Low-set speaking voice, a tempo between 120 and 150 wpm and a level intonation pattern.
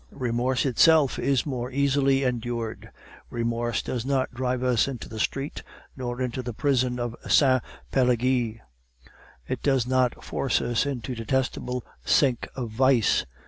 Yes: low, 125 Hz; average, 145 wpm; narrow, 1.9 semitones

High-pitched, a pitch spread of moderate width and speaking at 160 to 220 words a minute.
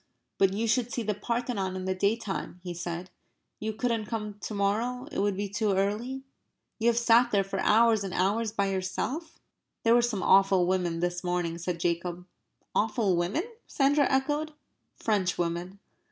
Yes: high, 205 Hz; average, 3.9 semitones; average, 170 wpm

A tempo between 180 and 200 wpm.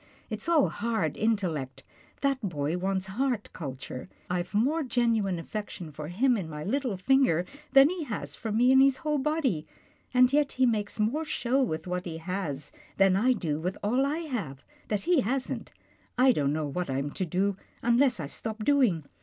Yes: average, 185 wpm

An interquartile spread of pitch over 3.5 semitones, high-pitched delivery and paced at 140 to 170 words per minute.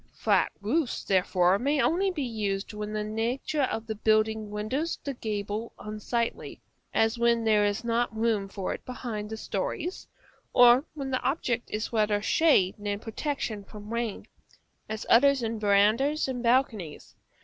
No: average, 3.2 semitones; high, 225 Hz; average, 155 wpm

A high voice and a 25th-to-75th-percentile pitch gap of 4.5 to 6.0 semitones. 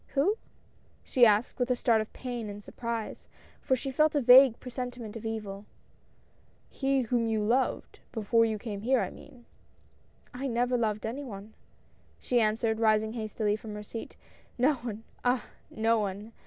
No: high, 230 Hz; narrow, 2.5 semitones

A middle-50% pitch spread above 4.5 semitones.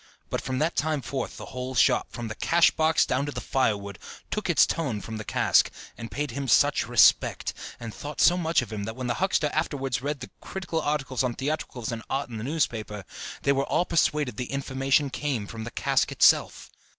No: average, 4.0 semitones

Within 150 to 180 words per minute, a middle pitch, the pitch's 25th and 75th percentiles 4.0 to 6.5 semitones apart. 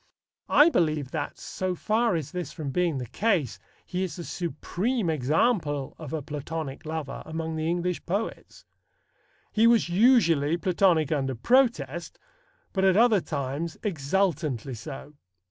No: average, 140 wpm; medium, 165 Hz; average, 4.8 semitones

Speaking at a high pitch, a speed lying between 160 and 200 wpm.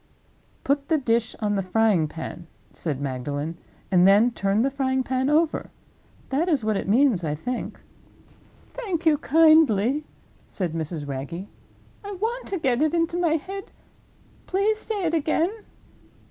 No: very high, 260 Hz; average, 150 wpm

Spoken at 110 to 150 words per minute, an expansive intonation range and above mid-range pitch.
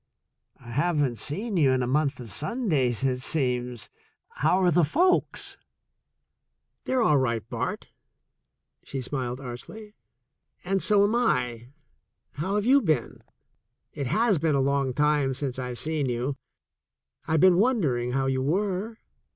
No: average, 145 wpm; wide, 6.7 semitones; medium, 145 Hz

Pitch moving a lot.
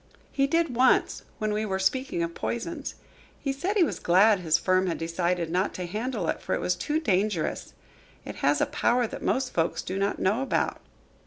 Yes: wide, 6.5 semitones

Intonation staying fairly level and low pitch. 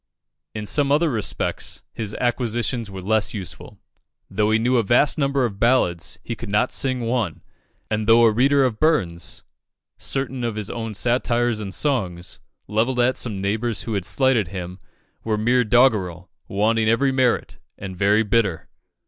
No: average, 3.5 semitones; low, 115 Hz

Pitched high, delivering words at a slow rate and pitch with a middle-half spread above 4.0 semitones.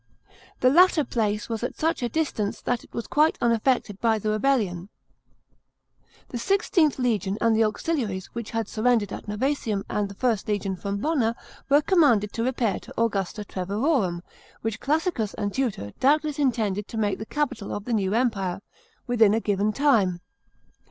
No: high, 225 Hz; average, 175 wpm; average, 4.4 semitones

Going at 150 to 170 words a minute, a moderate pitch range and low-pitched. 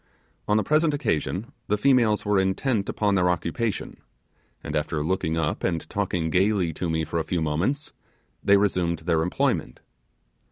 Yes: average, 160 wpm; average, 4.4 semitones; very low, 95 Hz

